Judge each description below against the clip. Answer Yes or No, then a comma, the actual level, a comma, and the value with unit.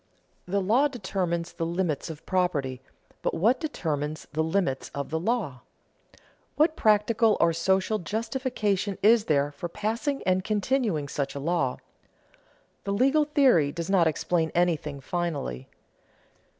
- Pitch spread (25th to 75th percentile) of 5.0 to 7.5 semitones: Yes, wide, 5.6 semitones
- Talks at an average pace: No, slow, 130 wpm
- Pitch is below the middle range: No, medium, 180 Hz